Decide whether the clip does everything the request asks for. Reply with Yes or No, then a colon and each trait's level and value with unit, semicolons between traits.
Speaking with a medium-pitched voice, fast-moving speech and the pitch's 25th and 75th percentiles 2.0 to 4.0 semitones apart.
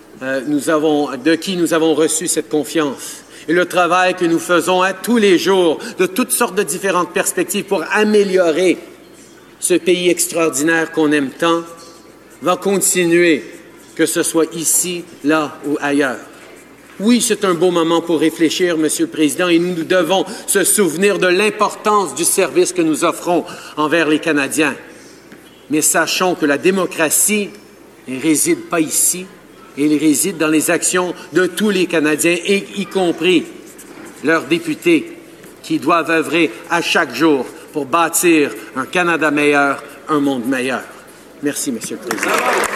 No: medium, 170 Hz; average, 155 wpm; average, 3.5 semitones